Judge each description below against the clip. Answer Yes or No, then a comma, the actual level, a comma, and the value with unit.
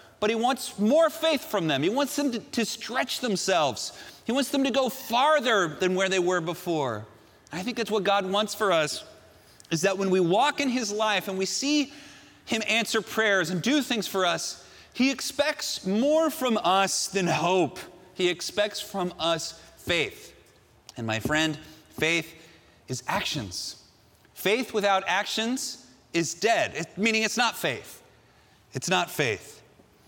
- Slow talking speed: No, average, 165 wpm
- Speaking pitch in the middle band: No, high, 200 Hz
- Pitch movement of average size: No, wide, 6.9 semitones